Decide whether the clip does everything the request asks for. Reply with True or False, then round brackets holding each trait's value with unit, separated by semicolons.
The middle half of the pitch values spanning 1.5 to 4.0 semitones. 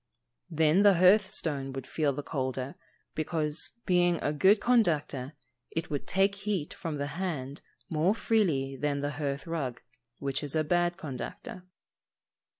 False (4.4 semitones)